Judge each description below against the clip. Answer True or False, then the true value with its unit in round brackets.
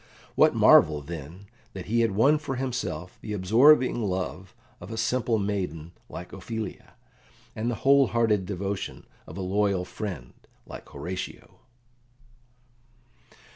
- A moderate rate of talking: False (130 wpm)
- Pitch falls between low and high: False (100 Hz)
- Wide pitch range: False (4.2 semitones)